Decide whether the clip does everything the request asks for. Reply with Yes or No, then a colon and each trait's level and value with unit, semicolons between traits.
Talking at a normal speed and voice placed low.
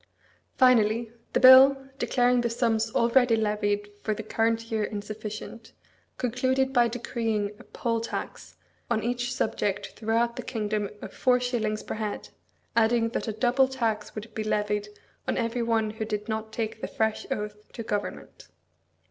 No: average, 155 wpm; high, 225 Hz